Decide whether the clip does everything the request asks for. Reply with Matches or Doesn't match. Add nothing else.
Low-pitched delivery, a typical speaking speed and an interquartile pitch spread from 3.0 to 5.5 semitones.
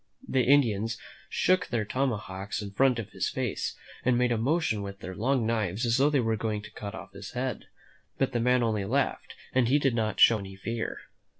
Doesn't match